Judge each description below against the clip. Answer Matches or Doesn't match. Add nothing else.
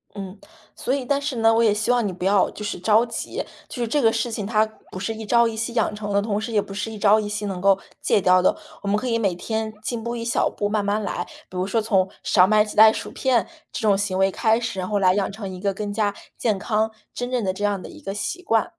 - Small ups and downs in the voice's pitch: Matches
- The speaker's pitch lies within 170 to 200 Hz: Doesn't match